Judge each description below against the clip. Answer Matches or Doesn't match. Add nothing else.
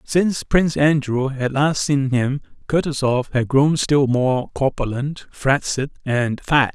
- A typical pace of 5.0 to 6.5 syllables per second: Doesn't match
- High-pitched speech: Doesn't match